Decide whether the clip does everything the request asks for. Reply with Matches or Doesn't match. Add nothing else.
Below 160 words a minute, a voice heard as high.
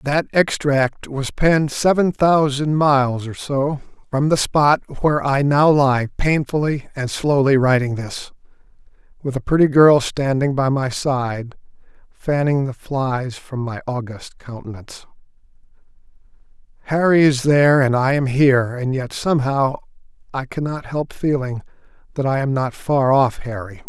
Doesn't match